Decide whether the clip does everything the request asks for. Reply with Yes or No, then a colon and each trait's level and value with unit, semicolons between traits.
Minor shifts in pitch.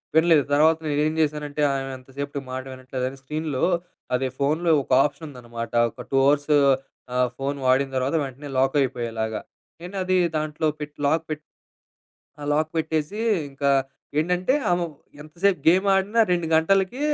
No: average, 3.2 semitones